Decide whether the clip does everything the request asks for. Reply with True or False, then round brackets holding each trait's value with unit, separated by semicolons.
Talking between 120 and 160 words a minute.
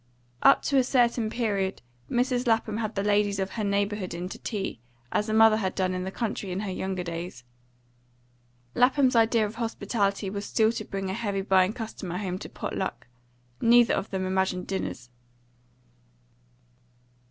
False (170 wpm)